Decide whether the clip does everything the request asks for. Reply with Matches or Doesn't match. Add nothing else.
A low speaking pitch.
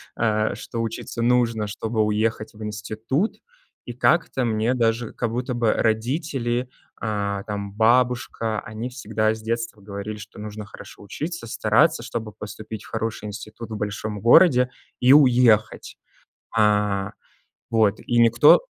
Matches